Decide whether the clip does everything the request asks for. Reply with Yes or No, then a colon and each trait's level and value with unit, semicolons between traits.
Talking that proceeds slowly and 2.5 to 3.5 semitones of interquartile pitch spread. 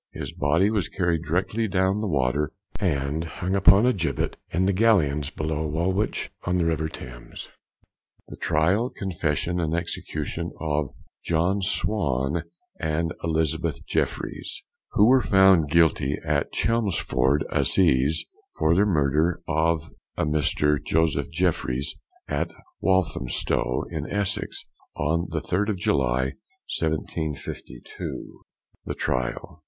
No: slow, 120 wpm; average, 4.2 semitones